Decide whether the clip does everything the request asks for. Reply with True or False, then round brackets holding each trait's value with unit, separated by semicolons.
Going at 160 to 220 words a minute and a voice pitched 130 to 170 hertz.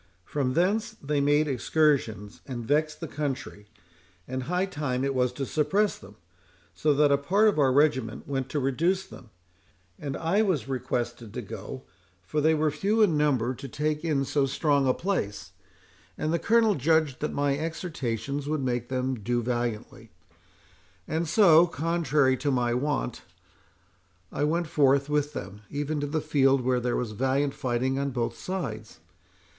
True (165 wpm; 140 Hz)